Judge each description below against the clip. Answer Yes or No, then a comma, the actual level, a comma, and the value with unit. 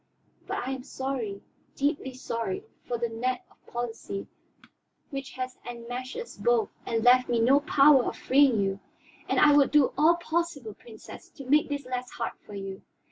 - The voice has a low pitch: No, very high, 255 Hz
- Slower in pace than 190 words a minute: Yes, average, 175 wpm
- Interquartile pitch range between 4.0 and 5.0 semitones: No, average, 3.5 semitones